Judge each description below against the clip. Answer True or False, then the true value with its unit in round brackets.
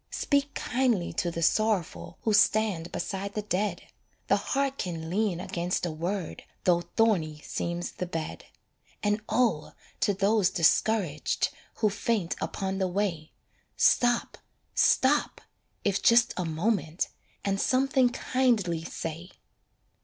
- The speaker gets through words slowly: True (125 wpm)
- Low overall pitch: False (195 Hz)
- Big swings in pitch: False (4.4 semitones)